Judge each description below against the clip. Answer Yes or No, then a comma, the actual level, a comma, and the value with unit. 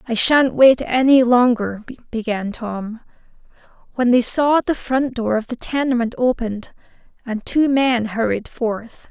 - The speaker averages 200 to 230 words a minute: No, average, 145 wpm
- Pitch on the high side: Yes, high, 240 Hz